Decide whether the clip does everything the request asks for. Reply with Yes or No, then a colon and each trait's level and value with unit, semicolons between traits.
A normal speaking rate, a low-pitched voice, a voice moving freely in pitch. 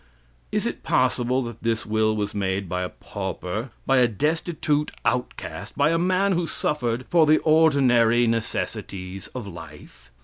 Yes: average, 150 wpm; low, 120 Hz; wide, 6.7 semitones